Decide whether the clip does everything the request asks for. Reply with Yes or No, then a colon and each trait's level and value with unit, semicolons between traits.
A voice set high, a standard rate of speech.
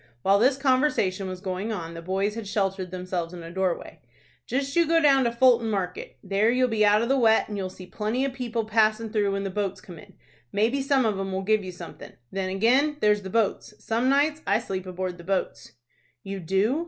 No: high, 210 Hz; fast, 225 wpm